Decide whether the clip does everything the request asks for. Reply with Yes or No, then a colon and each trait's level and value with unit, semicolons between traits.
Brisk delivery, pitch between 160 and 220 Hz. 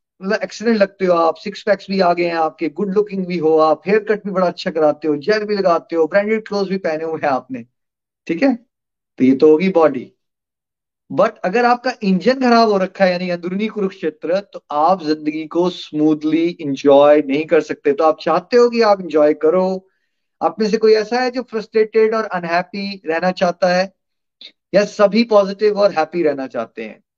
Yes: fast, 200 wpm; medium, 185 Hz